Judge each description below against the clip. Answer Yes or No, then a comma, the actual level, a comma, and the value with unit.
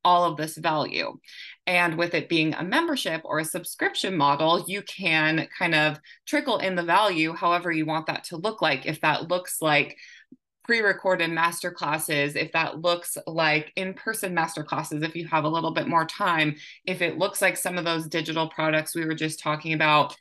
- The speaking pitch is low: No, medium, 165 Hz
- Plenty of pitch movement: No, narrow, 2.4 semitones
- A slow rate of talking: No, average, 195 wpm